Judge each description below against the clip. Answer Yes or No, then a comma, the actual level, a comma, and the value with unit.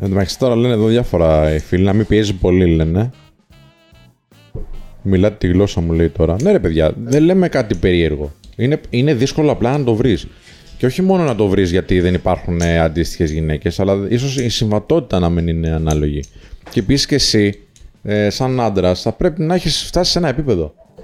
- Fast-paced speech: Yes, fast, 190 wpm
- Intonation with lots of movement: Yes, wide, 6.8 semitones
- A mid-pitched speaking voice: No, low, 100 Hz